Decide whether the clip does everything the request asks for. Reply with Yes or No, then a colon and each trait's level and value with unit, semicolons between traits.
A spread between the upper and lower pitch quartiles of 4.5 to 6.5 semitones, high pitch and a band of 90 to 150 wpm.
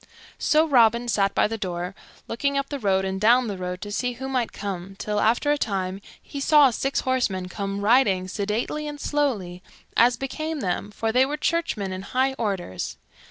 No: wide, 5.6 semitones; high, 225 Hz; average, 190 wpm